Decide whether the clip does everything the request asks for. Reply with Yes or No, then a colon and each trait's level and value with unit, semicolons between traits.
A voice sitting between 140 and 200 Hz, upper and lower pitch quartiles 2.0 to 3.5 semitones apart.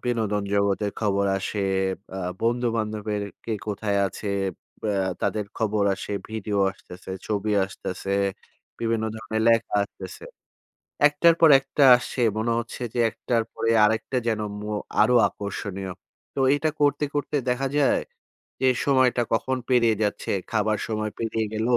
No: low, 110 Hz; average, 2.8 semitones